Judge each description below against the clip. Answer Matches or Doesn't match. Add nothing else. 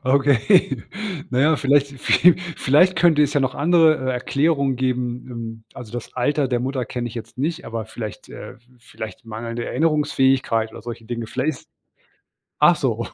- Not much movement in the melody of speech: Doesn't match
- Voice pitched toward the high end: Doesn't match